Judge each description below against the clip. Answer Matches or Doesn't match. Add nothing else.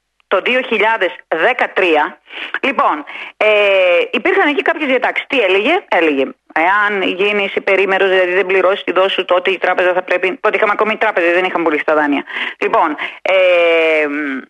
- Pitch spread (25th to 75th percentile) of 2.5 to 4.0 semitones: Matches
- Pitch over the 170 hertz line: Matches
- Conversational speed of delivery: Matches